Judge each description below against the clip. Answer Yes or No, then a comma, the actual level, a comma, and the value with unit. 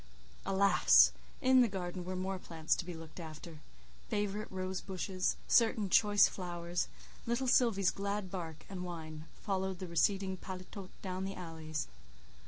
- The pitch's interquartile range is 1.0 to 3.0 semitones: Yes, average, 2.7 semitones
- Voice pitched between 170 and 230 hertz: Yes, medium, 185 Hz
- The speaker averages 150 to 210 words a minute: No, average, 140 wpm